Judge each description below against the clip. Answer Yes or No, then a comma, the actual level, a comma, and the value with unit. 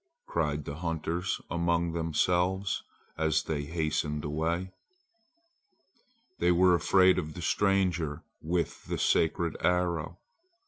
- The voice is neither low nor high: No, very low, 85 Hz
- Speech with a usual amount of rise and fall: No, narrow, 2.3 semitones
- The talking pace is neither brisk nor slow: No, slow, 105 wpm